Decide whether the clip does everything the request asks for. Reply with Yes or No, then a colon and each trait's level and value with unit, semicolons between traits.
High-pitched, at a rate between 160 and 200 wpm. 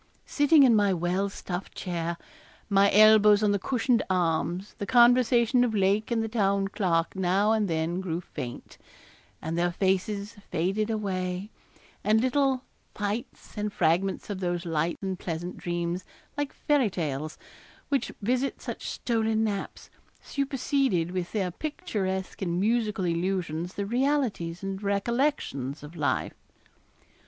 No: high, 200 Hz; slow, 135 wpm